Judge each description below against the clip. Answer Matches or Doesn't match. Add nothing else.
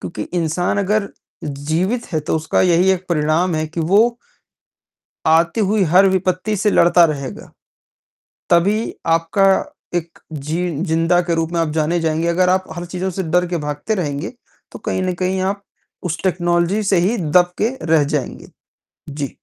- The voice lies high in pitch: Doesn't match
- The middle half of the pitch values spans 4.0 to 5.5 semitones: Doesn't match